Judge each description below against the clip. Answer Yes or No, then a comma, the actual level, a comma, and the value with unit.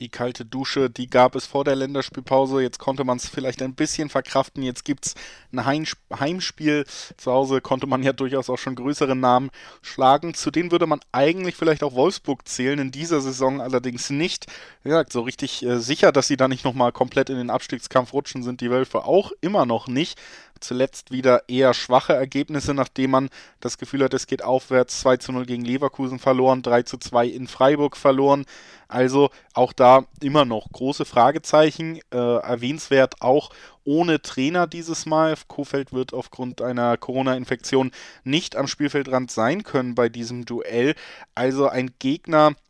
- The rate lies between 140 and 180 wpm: Yes, average, 175 wpm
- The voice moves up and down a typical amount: No, narrow, 2.0 semitones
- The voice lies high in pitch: No, low, 130 Hz